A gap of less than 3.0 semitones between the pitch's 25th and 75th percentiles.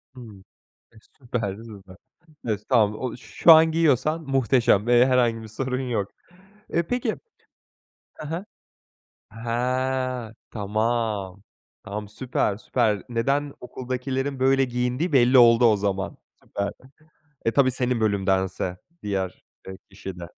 No: average, 4.0 semitones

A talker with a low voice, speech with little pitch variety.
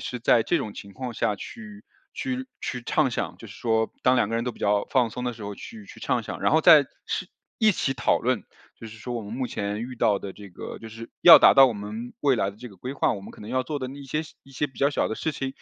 No: low, 120 Hz; average, 4.0 semitones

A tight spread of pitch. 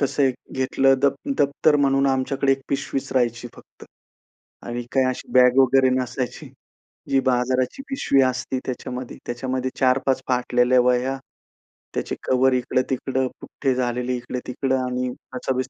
Yes: narrow, 1.2 semitones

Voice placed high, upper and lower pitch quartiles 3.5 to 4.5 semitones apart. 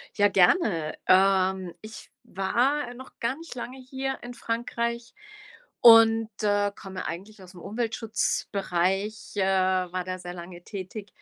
Yes: high, 205 Hz; average, 4.1 semitones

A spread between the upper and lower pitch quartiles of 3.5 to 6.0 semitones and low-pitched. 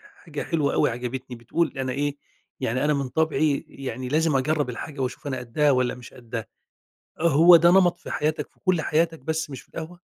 No: average, 3.8 semitones; medium, 145 Hz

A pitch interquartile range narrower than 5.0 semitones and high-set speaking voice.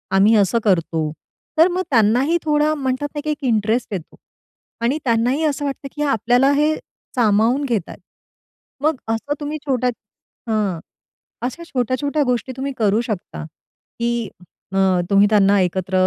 No: average, 5.3 semitones; high, 240 Hz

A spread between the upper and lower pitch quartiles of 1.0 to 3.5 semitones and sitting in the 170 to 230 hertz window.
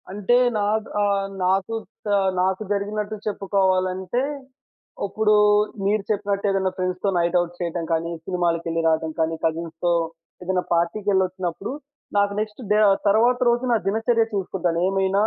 Yes: average, 2.8 semitones; high, 190 Hz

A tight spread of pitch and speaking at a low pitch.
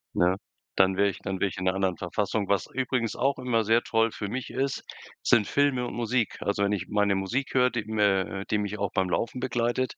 No: average, 4.0 semitones; low, 105 Hz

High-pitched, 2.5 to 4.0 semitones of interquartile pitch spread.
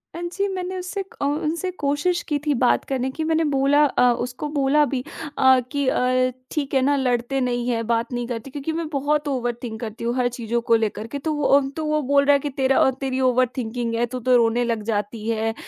Yes: very high, 260 Hz; average, 3.4 semitones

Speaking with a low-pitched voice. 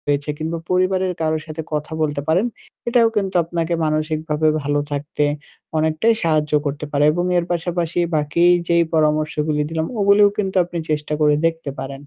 No: medium, 160 Hz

